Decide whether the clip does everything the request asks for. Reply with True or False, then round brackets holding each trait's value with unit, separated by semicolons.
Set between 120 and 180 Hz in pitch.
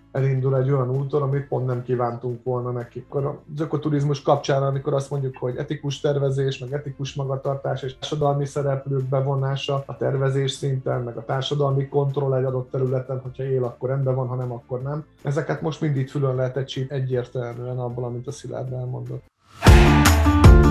True (135 Hz)